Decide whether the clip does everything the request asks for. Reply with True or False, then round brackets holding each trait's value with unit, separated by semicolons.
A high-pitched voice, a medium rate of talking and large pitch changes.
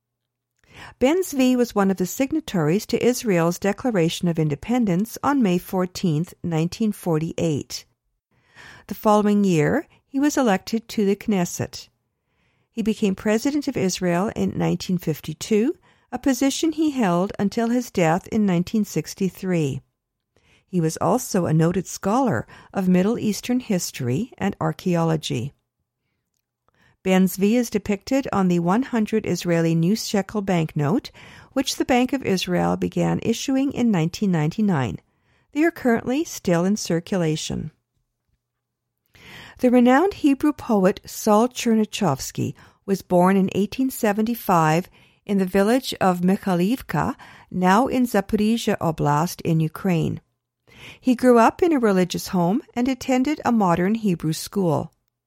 False (195 Hz; 125 wpm; 5.8 semitones)